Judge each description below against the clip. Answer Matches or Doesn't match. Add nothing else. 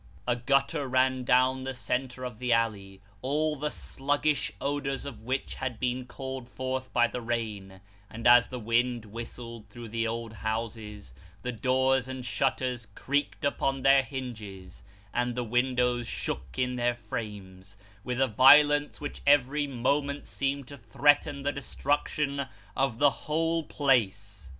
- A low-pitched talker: Matches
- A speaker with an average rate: Matches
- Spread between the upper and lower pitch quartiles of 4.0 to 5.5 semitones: Doesn't match